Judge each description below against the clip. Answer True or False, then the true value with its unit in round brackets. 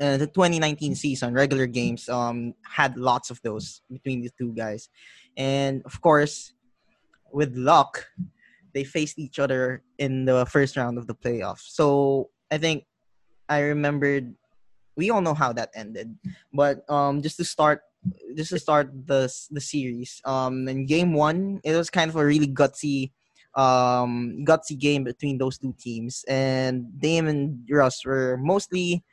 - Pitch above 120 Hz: True (140 Hz)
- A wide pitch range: False (3.1 semitones)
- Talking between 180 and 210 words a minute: False (160 wpm)